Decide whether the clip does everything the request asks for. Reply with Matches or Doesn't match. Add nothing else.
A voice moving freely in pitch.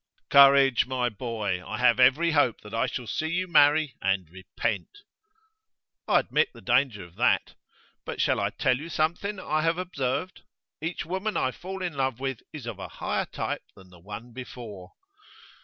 Matches